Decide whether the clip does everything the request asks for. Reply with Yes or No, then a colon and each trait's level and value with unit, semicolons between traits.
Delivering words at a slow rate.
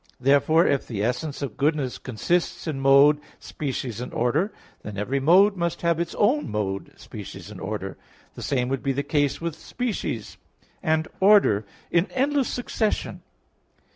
No: average, 155 wpm